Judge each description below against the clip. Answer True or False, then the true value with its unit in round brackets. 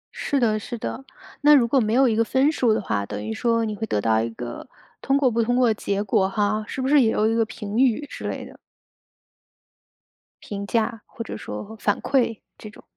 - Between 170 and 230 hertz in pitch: True (225 Hz)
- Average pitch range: True (3.4 semitones)